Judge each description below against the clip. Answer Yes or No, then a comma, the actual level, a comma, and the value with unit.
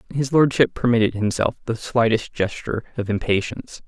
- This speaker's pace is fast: No, average, 140 wpm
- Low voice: Yes, low, 115 Hz